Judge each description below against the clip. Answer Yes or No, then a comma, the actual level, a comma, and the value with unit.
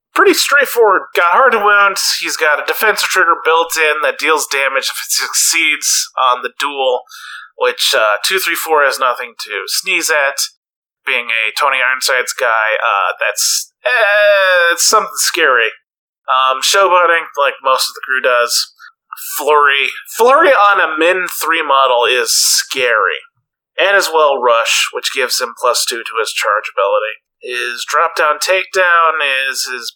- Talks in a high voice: Yes, high, 200 Hz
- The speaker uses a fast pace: No, average, 160 wpm